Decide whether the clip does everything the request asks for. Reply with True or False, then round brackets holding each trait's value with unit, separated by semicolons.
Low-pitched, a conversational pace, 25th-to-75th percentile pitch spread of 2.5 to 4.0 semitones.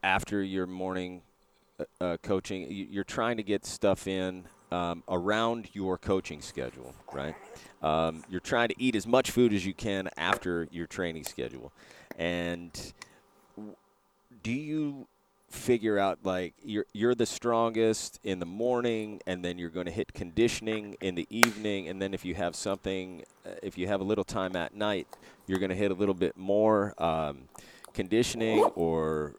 True (95 Hz; 165 wpm; 3.4 semitones)